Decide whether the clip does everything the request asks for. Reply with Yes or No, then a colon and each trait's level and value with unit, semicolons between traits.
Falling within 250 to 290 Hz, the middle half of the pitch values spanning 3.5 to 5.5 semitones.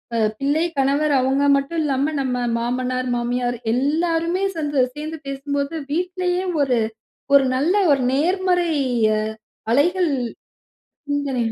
Yes: very high, 285 Hz; average, 4.2 semitones